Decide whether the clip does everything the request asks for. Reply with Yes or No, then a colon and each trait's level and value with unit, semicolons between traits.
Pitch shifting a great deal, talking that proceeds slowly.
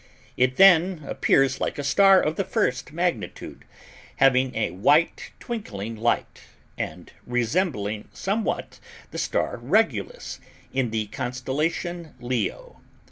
Yes: wide, 6.8 semitones; slow, 115 wpm